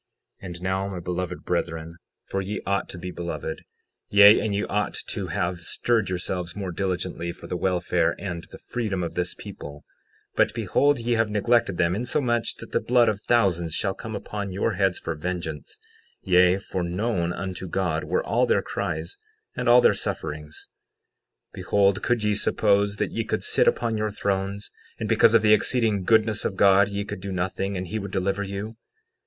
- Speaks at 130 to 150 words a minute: No, average, 185 wpm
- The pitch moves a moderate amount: Yes, average, 3.0 semitones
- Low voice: Yes, very low, 95 Hz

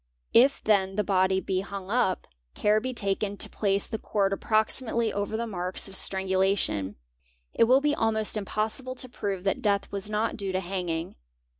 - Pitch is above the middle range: Yes, high, 200 Hz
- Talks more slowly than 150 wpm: No, average, 175 wpm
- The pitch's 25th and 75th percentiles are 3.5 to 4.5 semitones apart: No, narrow, 2.5 semitones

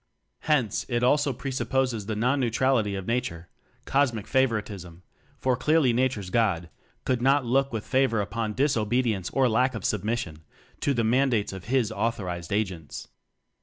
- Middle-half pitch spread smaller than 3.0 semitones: No, average, 4.1 semitones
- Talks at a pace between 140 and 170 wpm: Yes, average, 155 wpm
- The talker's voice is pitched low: Yes, low, 115 Hz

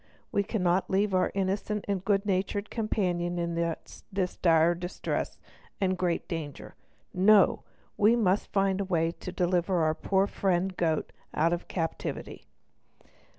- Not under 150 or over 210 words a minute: No, average, 140 wpm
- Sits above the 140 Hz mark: Yes, medium, 185 Hz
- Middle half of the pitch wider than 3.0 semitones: No, narrow, 2.4 semitones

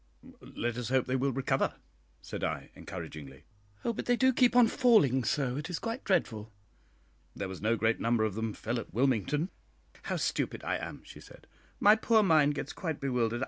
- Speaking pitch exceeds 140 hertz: No, low, 130 Hz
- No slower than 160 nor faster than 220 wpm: Yes, average, 190 wpm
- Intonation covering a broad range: Yes, wide, 8.8 semitones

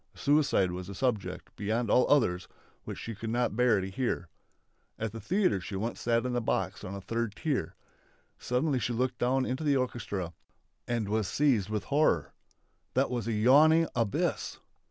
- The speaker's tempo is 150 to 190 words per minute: Yes, average, 175 wpm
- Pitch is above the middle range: No, low, 115 Hz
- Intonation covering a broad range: No, average, 4.2 semitones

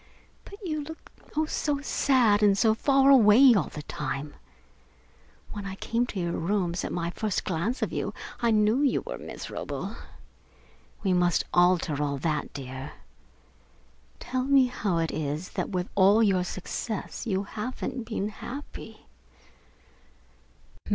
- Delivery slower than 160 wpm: Yes, average, 145 wpm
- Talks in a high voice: Yes, high, 205 Hz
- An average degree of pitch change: No, wide, 6.1 semitones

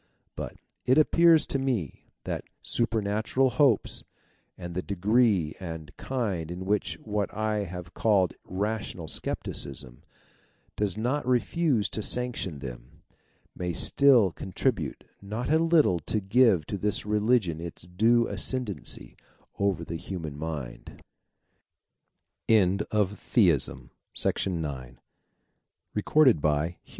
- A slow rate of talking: Yes, slow, 115 wpm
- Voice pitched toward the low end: Yes, low, 100 Hz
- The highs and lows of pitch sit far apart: Yes, wide, 5.7 semitones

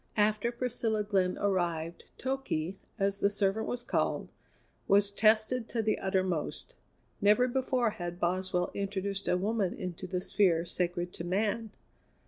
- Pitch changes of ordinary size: Yes, average, 3.3 semitones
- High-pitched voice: Yes, high, 200 Hz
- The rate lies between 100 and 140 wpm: Yes, slow, 135 wpm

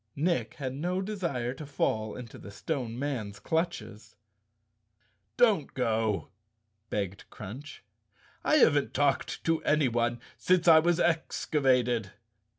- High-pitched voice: No, low, 135 Hz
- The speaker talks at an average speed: No, slow, 115 wpm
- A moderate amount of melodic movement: No, wide, 6.0 semitones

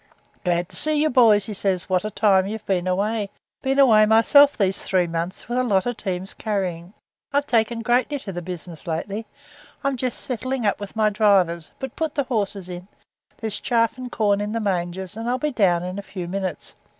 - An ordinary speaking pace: No, fast, 210 wpm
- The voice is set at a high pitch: Yes, high, 205 Hz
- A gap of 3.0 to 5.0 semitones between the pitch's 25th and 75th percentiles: Yes, average, 4.5 semitones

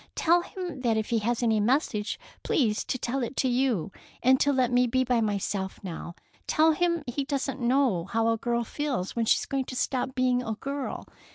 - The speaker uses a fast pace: Yes, fast, 210 wpm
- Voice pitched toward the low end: No, very high, 250 Hz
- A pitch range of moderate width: Yes, average, 3.3 semitones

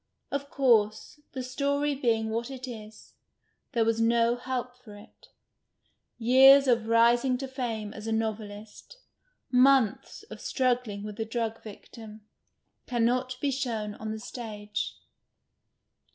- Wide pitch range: No, average, 2.8 semitones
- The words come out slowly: Yes, slow, 130 wpm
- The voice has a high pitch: Yes, high, 235 Hz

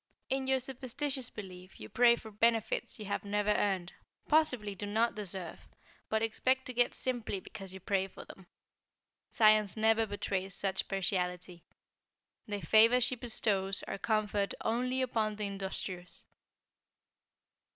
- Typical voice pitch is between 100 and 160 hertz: No, high, 210 Hz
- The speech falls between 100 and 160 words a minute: Yes, average, 140 wpm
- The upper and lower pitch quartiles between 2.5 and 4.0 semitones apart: Yes, average, 3.4 semitones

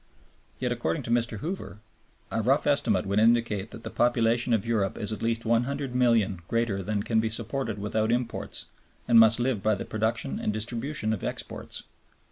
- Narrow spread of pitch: Yes, narrow, 1.8 semitones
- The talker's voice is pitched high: No, low, 115 Hz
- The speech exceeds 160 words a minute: Yes, average, 175 wpm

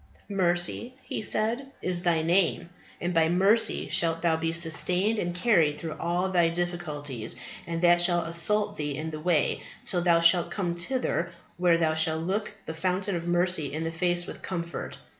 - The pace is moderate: Yes, average, 175 wpm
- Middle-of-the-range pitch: Yes, medium, 175 Hz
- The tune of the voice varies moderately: No, narrow, 1.8 semitones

